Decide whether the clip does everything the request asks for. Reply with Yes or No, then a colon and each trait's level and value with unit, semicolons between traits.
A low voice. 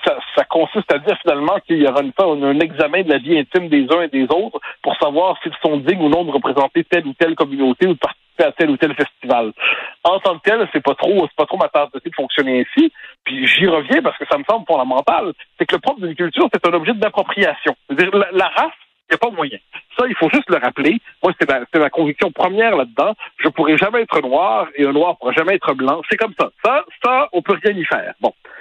No: medium, 165 Hz